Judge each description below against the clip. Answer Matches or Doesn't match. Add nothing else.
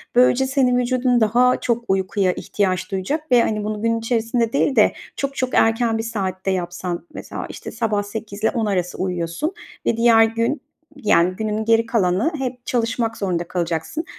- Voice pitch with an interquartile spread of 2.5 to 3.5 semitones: Doesn't match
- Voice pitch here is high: Matches